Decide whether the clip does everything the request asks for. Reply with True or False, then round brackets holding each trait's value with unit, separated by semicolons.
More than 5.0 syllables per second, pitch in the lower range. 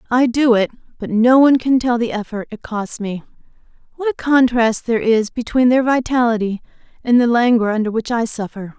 False (5.5 syllables/s; 235 Hz)